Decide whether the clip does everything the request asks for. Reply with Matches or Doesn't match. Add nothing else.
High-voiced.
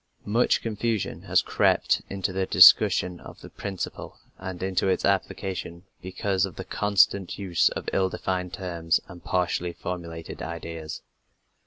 Doesn't match